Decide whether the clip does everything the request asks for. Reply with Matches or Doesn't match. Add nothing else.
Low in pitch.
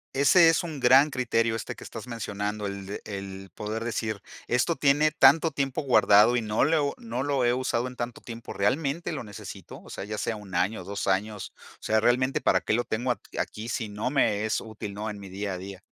Matches